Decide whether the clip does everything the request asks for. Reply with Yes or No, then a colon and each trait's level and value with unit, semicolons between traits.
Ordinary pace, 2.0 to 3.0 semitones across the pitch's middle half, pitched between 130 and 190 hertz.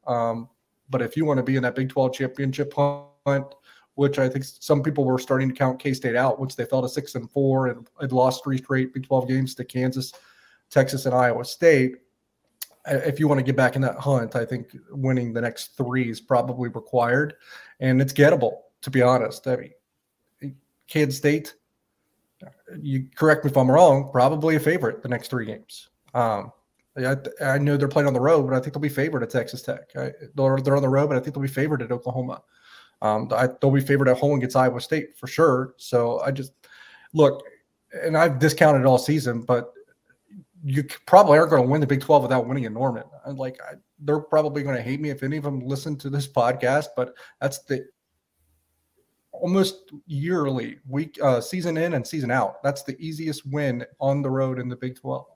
No: fast, 210 wpm; narrow, 2.4 semitones; low, 135 Hz